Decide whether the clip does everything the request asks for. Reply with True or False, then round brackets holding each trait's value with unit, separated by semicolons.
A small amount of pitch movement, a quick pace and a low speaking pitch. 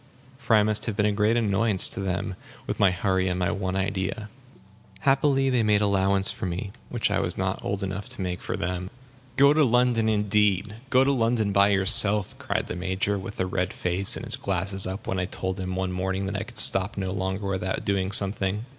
True (2.1 semitones; 215 wpm; 100 Hz)